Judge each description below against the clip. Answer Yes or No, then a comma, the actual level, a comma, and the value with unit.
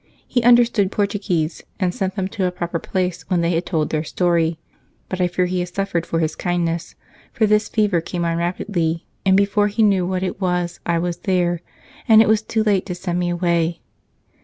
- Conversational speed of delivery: No, fast, 210 wpm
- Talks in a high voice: No, medium, 180 Hz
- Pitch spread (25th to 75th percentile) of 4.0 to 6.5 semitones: No, average, 2.7 semitones